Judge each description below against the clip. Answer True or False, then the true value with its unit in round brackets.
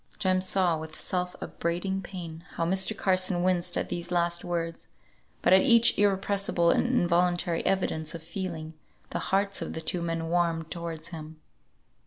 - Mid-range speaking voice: True (175 Hz)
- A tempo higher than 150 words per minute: True (160 wpm)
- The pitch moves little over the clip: True (2.2 semitones)